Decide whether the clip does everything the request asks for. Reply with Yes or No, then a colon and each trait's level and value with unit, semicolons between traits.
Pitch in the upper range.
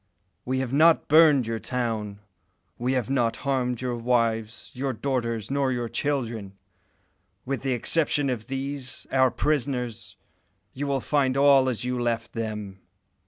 No: low, 125 Hz